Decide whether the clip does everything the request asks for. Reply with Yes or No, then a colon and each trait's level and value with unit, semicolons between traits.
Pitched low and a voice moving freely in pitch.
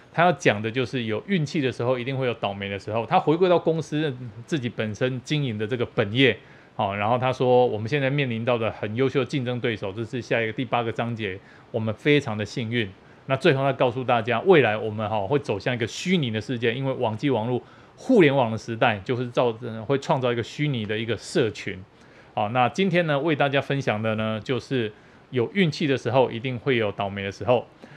No: low, 125 Hz; average, 3.7 semitones